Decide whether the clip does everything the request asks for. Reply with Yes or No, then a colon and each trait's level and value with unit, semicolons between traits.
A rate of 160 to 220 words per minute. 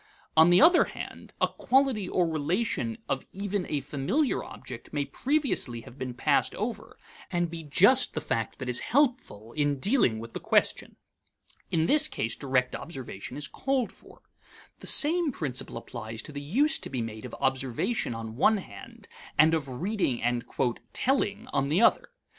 Yes: average, 170 wpm